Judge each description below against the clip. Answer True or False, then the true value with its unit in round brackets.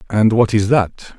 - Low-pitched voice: True (110 Hz)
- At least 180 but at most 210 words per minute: True (205 wpm)